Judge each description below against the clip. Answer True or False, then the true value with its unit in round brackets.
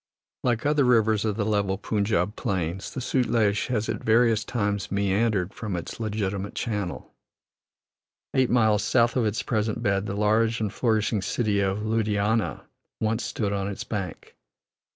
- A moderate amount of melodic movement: False (2.1 semitones)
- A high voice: False (105 Hz)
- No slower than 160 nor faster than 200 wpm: False (150 wpm)